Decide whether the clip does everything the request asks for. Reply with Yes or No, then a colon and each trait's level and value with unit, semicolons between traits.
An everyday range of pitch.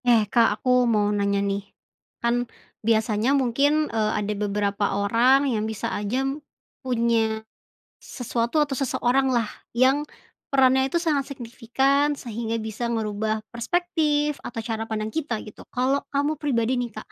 Yes: average, 3.7 semitones